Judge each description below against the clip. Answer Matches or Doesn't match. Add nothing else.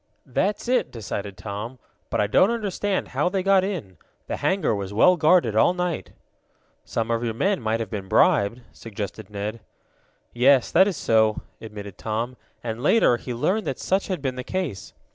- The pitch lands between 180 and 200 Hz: Doesn't match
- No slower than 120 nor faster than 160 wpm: Doesn't match